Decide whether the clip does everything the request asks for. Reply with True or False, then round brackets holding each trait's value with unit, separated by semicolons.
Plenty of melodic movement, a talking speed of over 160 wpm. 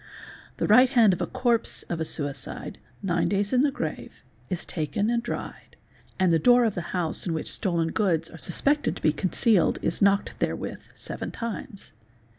True (5.7 semitones; 190 wpm)